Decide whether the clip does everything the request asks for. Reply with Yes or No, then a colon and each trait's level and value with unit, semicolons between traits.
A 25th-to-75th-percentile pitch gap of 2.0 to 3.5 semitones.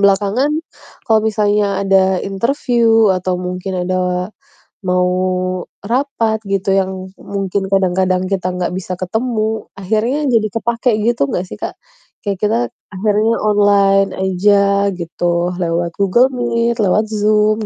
Yes: average, 2.9 semitones